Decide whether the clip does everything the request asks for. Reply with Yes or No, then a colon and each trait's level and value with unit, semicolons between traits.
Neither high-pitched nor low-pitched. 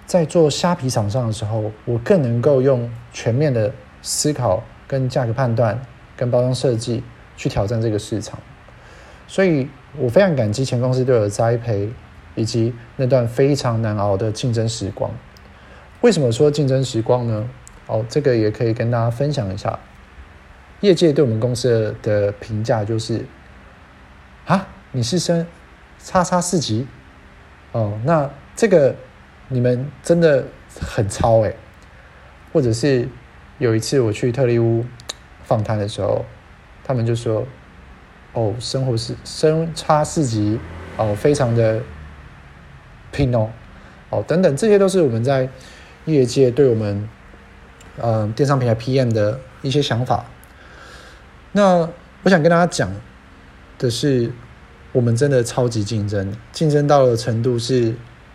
No: low, 115 Hz